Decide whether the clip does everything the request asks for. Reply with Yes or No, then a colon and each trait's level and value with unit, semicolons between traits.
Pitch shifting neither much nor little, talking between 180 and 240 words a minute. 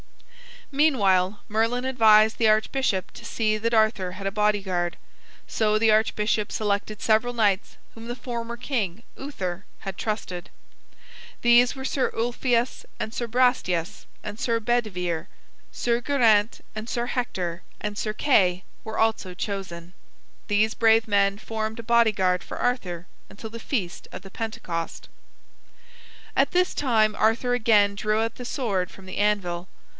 No: average, 3.2 semitones; average, 145 wpm